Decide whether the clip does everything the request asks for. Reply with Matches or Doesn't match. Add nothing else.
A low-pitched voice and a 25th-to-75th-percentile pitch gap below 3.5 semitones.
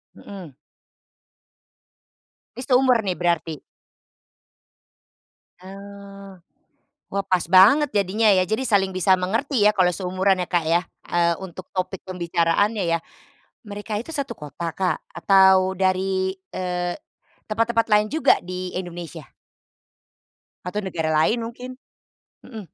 Doesn't match